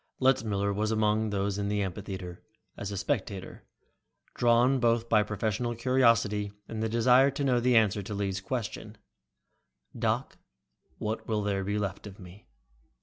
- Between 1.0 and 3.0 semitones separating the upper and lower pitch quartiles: Yes, average, 2.7 semitones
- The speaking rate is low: No, average, 150 wpm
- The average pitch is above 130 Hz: No, low, 105 Hz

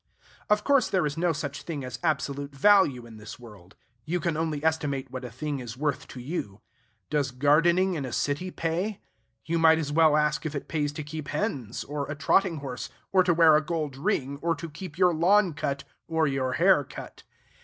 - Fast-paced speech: Yes, fast, 210 wpm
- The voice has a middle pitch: Yes, medium, 150 Hz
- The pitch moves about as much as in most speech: Yes, average, 3.3 semitones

